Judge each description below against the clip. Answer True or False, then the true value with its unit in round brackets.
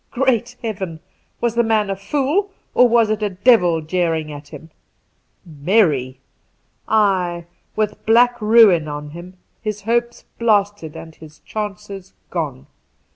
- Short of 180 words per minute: True (135 wpm)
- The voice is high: True (200 Hz)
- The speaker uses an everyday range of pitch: False (5.7 semitones)